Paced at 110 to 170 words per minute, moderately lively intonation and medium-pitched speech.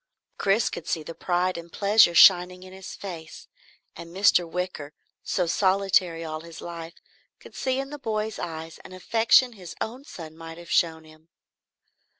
Yes: average, 165 wpm; average, 3.3 semitones; medium, 180 Hz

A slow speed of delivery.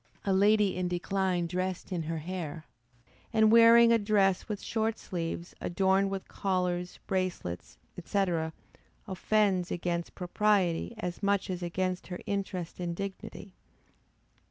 Yes: slow, 130 wpm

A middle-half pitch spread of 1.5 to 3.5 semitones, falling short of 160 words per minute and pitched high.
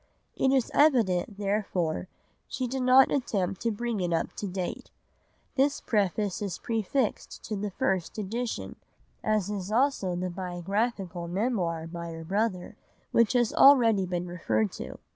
No: average, 4.6 semitones; average, 145 wpm; high, 200 Hz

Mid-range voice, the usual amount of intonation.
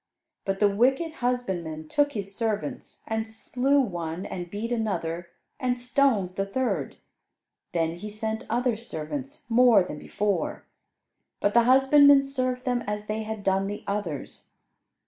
No: high, 220 Hz; average, 4.5 semitones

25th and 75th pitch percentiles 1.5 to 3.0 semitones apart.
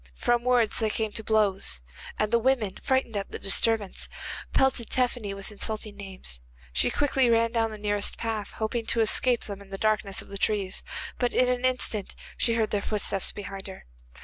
Yes: average, 2.7 semitones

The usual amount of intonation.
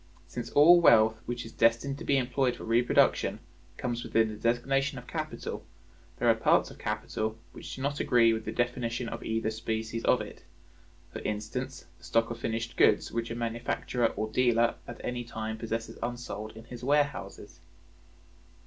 No: narrow, 1.7 semitones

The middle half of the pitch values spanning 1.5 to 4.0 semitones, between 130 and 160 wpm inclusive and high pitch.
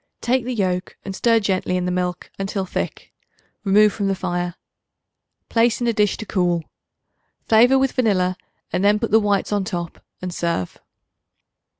No: average, 3.5 semitones; average, 170 wpm; high, 195 Hz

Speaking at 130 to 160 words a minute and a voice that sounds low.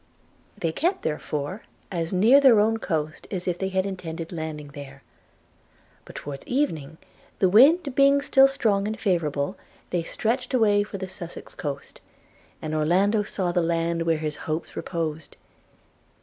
No: average, 155 wpm; medium, 180 Hz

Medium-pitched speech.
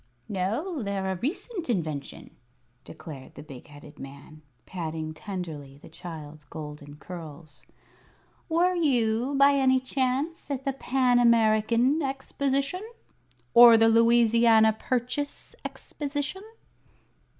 No: high, 230 Hz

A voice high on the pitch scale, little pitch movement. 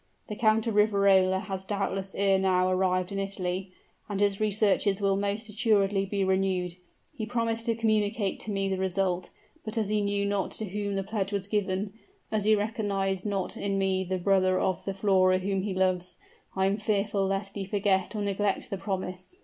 Yes: high, 195 Hz; narrow, 1.6 semitones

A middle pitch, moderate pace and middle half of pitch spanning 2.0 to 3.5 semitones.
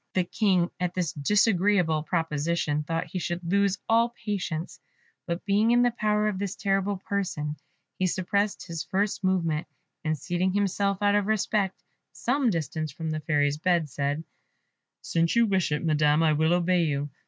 No: medium, 180 Hz; average, 165 wpm; average, 4.1 semitones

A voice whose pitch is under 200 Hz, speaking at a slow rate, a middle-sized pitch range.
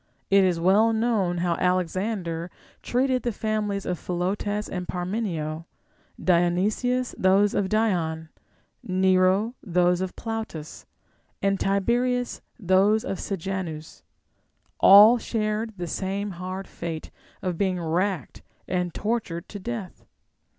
Yes: high, 190 Hz; slow, 115 wpm; average, 3.4 semitones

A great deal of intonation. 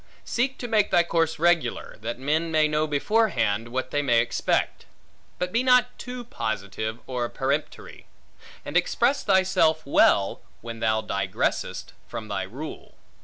Yes: wide, 8.5 semitones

